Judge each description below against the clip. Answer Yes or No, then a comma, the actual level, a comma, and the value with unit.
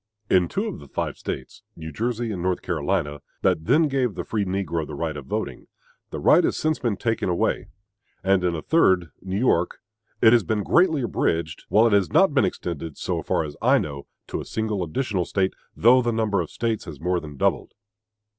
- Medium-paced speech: No, fast, 210 wpm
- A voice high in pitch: No, very low, 95 Hz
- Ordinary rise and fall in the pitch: No, wide, 5.7 semitones